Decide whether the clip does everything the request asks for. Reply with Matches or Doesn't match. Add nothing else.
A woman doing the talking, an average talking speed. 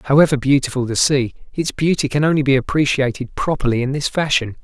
Doesn't match